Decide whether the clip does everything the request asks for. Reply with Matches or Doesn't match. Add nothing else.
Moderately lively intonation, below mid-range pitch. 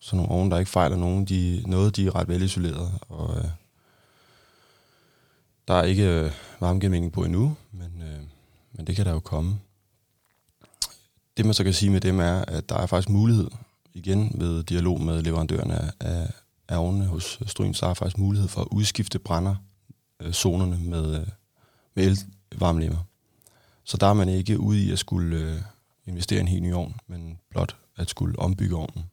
Matches